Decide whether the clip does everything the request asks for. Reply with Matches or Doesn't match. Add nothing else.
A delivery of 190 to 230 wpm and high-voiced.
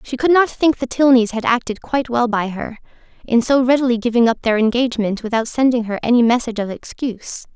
Matches